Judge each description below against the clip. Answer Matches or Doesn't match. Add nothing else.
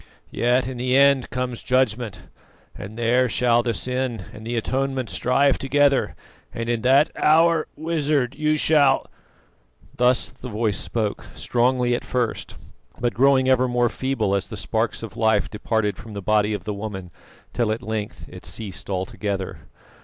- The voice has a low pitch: Matches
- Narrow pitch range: Doesn't match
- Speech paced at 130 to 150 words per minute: Doesn't match